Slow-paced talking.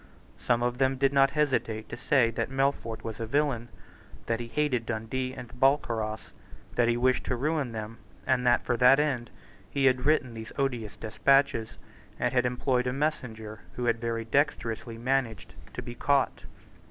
No: average, 175 wpm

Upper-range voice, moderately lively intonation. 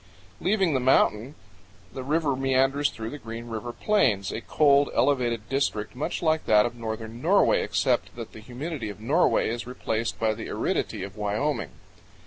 No: low, 120 Hz; average, 4.3 semitones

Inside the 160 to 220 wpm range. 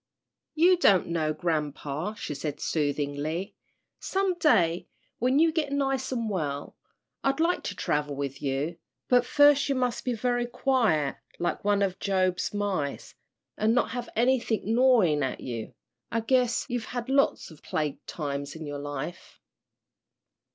No: average, 150 wpm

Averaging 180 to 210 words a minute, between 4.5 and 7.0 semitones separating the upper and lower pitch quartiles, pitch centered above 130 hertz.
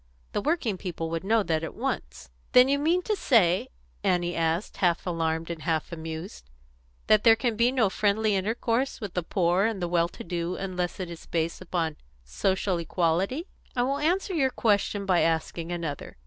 Yes: average, 185 wpm; average, 5.1 semitones; medium, 185 Hz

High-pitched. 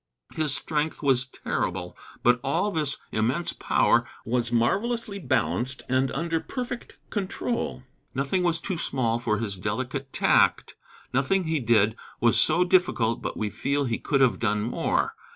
No: low, 135 Hz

